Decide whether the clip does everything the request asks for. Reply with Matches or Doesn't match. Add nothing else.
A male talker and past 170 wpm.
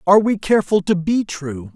Matches